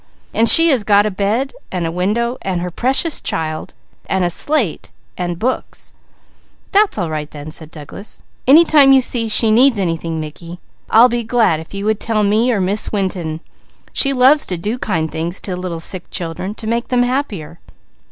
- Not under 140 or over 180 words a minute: No, average, 190 wpm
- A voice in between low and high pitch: No, high, 200 Hz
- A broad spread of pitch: Yes, wide, 6.1 semitones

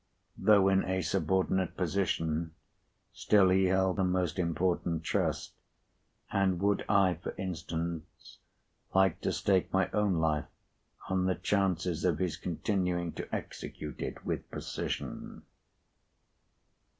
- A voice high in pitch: No, very low, 90 Hz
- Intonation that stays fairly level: Yes, narrow, 2.2 semitones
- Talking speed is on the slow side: Yes, slow, 120 wpm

